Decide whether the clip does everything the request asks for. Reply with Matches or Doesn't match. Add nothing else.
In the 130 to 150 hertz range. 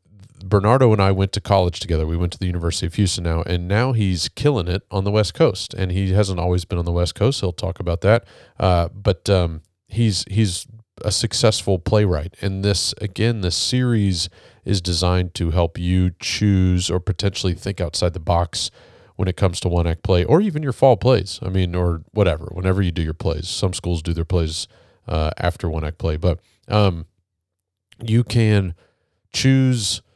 Doesn't match